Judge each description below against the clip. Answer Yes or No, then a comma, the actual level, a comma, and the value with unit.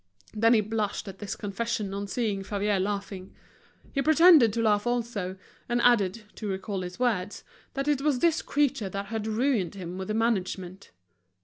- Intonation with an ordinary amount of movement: Yes, average, 3.6 semitones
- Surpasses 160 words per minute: Yes, average, 175 wpm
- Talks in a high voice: Yes, high, 215 Hz